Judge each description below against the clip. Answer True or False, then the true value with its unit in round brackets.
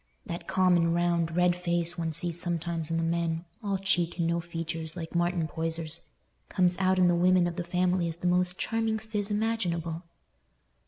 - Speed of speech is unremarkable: True (170 wpm)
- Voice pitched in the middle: True (175 Hz)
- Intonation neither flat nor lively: False (1.5 semitones)